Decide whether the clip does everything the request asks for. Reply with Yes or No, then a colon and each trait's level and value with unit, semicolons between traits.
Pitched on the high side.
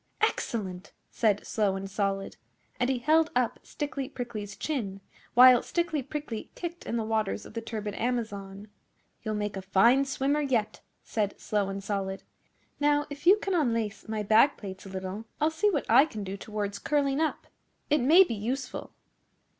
Yes: high, 230 Hz